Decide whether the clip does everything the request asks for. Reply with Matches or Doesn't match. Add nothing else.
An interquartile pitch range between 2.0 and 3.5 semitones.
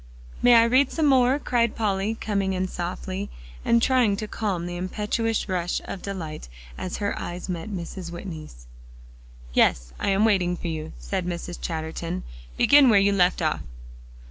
Doesn't match